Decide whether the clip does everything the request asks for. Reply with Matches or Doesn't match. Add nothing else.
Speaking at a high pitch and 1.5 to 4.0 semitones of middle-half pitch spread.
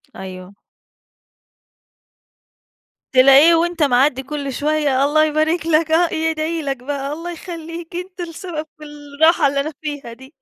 Matches